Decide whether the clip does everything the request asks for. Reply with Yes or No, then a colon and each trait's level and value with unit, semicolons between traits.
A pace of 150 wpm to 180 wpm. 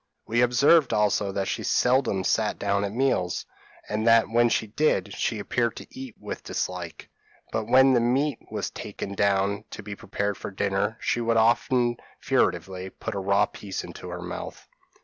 Yes: average, 175 wpm